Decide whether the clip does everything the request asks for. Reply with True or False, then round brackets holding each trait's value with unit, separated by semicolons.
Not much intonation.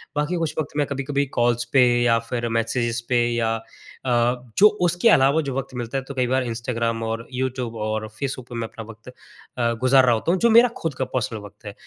False (3.2 semitones)